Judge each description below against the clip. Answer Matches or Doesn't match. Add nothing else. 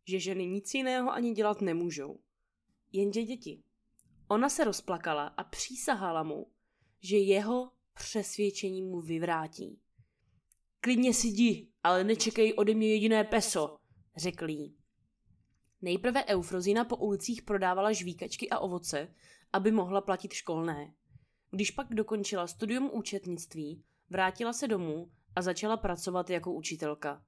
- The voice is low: Doesn't match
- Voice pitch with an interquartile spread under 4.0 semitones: Doesn't match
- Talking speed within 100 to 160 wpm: Matches